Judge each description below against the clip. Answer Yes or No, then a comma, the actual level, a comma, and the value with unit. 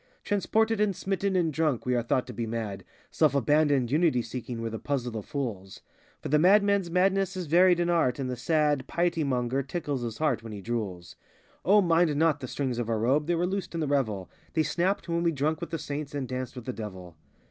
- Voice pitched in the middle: Yes, medium, 145 Hz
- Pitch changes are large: Yes, wide, 6.0 semitones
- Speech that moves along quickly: Yes, fast, 225 wpm